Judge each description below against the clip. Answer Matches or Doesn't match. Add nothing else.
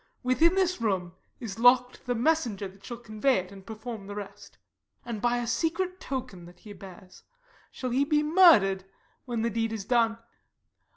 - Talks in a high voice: Matches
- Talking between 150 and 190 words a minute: Matches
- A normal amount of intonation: Matches